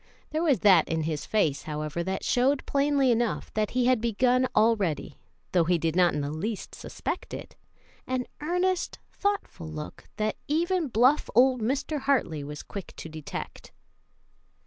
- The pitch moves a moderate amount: No, wide, 8.7 semitones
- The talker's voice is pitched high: Yes, high, 225 Hz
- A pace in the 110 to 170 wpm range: Yes, average, 160 wpm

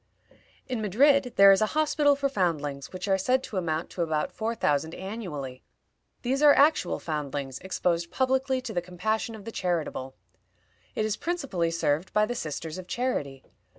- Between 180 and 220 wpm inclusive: No, average, 170 wpm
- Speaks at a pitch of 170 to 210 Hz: Yes, high, 190 Hz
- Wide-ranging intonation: Yes, wide, 7.8 semitones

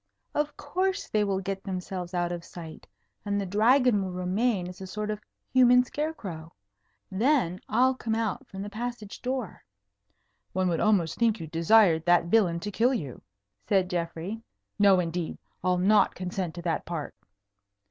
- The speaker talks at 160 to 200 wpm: Yes, average, 165 wpm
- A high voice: Yes, high, 195 Hz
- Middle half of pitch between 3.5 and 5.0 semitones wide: Yes, average, 4.3 semitones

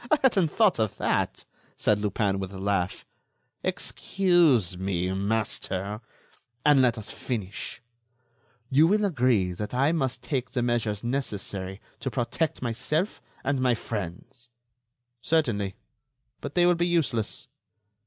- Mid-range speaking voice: No, low, 120 Hz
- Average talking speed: No, slow, 130 wpm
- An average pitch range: No, wide, 6.4 semitones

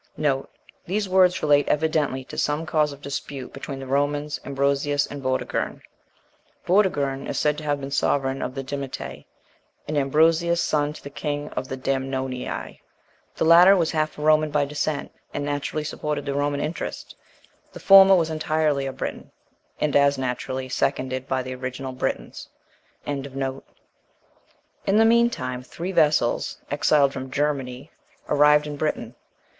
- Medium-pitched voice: Yes, medium, 145 Hz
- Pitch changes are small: Yes, narrow, 2.3 semitones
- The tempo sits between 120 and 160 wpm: Yes, average, 150 wpm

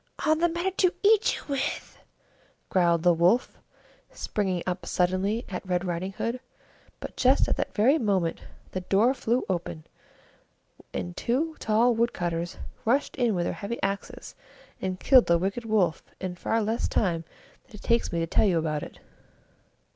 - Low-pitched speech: No, high, 200 Hz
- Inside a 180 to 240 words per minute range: No, average, 170 wpm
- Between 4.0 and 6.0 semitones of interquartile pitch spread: Yes, average, 5.2 semitones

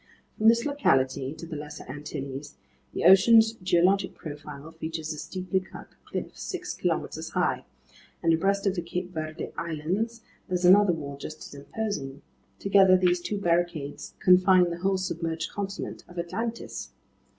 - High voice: No, medium, 175 Hz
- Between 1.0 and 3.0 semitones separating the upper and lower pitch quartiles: No, average, 3.9 semitones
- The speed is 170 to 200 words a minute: No, average, 150 wpm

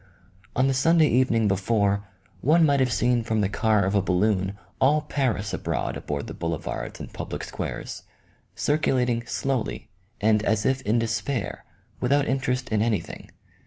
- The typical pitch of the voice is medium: No, low, 115 Hz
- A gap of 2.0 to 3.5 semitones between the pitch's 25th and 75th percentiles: No, average, 4.4 semitones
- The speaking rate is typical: Yes, average, 160 wpm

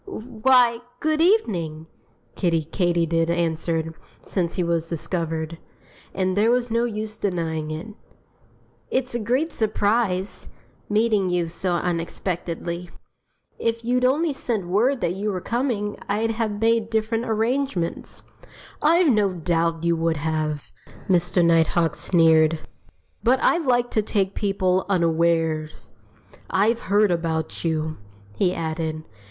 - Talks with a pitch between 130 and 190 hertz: Yes, medium, 185 Hz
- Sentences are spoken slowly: Yes, slow, 125 wpm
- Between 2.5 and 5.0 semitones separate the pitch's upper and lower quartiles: No, wide, 5.4 semitones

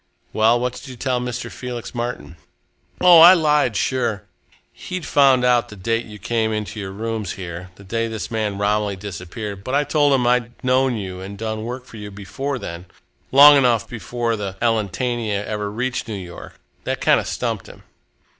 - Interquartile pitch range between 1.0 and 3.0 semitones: No, average, 3.5 semitones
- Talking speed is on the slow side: No, average, 190 wpm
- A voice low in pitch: Yes, low, 115 Hz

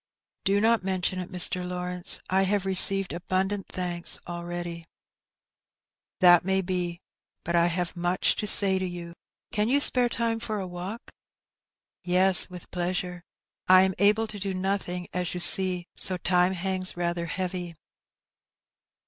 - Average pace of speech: Yes, average, 160 wpm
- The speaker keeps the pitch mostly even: Yes, narrow, 1.5 semitones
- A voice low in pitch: No, medium, 185 Hz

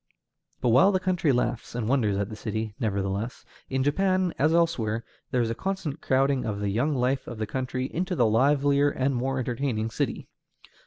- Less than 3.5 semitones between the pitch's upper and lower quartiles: No, average, 4.2 semitones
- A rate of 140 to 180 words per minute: No, average, 190 wpm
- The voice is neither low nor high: No, low, 130 Hz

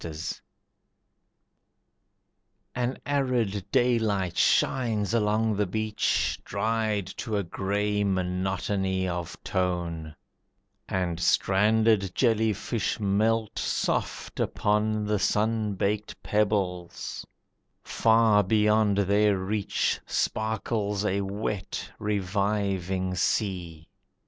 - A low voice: Yes, low, 105 Hz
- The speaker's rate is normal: No, slow, 85 wpm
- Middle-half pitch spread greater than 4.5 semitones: No, narrow, 2.4 semitones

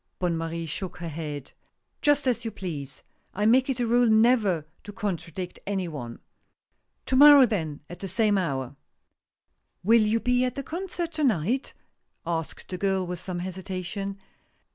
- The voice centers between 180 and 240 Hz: Yes, high, 190 Hz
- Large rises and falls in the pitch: Yes, wide, 6.1 semitones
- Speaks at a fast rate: No, average, 175 wpm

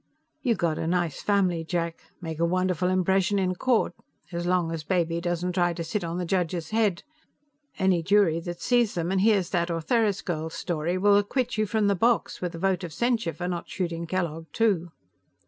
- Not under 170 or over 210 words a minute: Yes, average, 200 wpm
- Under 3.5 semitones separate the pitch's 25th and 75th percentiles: Yes, average, 2.9 semitones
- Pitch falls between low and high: Yes, medium, 180 Hz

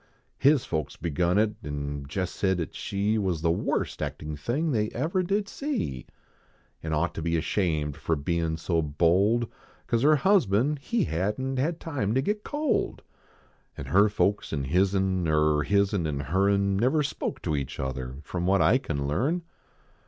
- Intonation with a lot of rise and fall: Yes, wide, 8.5 semitones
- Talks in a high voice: No, very low, 95 Hz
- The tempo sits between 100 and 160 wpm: No, average, 180 wpm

